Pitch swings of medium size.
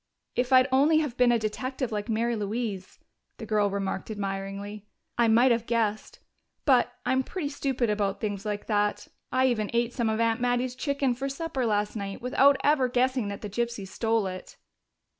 Yes: average, 3.6 semitones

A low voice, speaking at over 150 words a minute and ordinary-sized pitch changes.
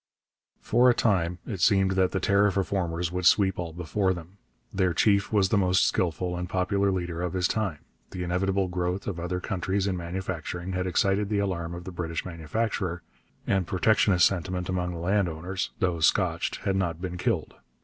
No: very low, 90 Hz; average, 180 wpm; narrow, 1.9 semitones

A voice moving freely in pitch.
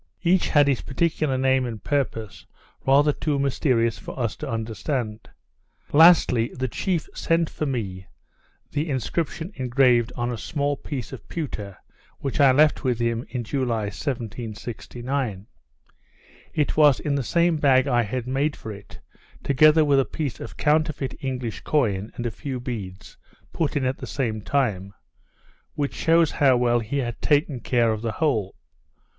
No: average, 3.9 semitones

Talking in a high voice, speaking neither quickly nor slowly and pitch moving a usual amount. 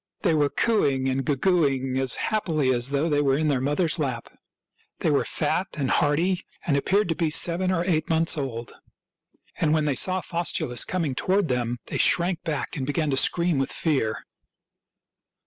No: medium, 150 Hz; average, 185 wpm; average, 4.3 semitones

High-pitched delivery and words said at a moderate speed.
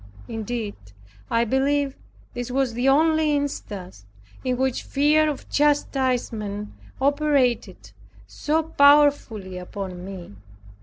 No: very high, 260 Hz; slow, 100 wpm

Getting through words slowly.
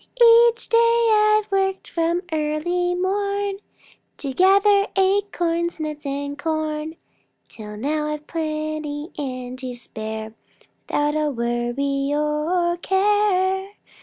Yes: slow, 110 wpm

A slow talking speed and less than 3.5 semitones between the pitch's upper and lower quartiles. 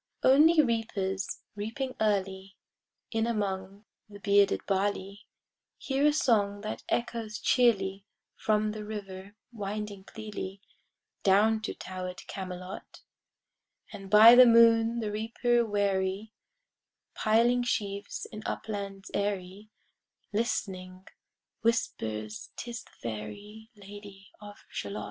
Yes: slow, 105 wpm; narrow, 2.6 semitones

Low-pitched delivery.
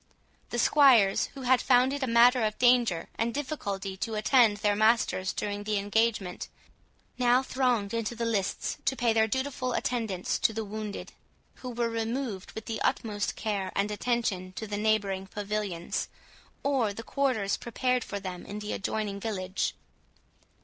No: high, 220 Hz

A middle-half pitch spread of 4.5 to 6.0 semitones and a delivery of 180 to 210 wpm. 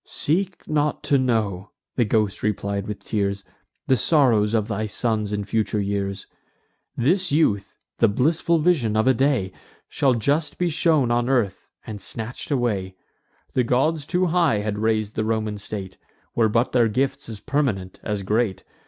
No: average, 5.1 semitones; average, 160 wpm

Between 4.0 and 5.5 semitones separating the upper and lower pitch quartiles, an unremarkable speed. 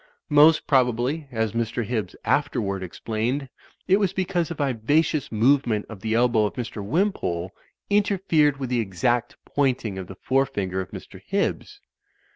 Yes: average, 5.2 semitones; average, 155 wpm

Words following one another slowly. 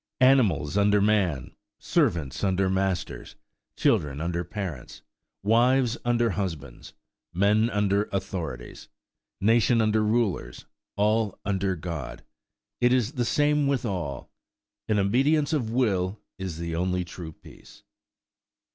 Yes: slow, 90 wpm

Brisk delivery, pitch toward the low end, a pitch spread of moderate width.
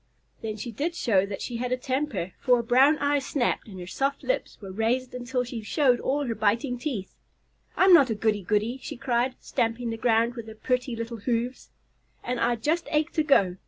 No: fast, 210 wpm; high, 245 Hz; average, 3.1 semitones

